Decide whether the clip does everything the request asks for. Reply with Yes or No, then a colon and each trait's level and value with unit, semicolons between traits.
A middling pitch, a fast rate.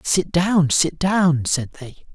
No: medium, 165 Hz; average, 170 wpm